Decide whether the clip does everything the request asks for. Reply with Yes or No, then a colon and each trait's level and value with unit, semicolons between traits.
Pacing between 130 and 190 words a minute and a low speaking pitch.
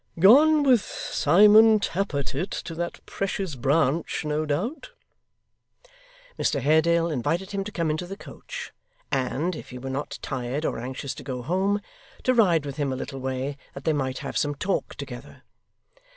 No: average, 165 wpm; medium, 160 Hz